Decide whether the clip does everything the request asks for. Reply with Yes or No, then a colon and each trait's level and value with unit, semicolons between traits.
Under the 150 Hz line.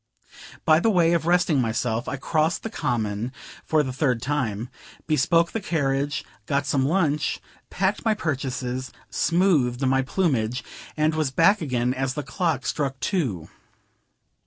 Yes: medium, 140 Hz